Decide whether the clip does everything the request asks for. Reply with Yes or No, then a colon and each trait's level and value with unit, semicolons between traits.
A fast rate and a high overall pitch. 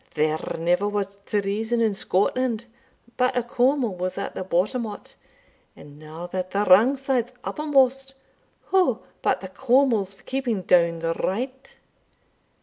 No: average, 145 wpm; high, 210 Hz